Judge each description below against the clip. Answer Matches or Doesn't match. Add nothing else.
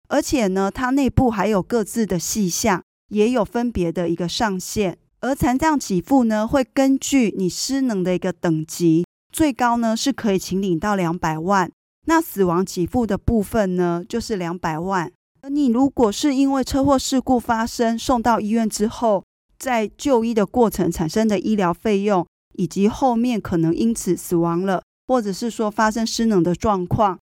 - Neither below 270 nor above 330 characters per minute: Doesn't match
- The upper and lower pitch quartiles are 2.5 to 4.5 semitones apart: Doesn't match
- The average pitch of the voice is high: Matches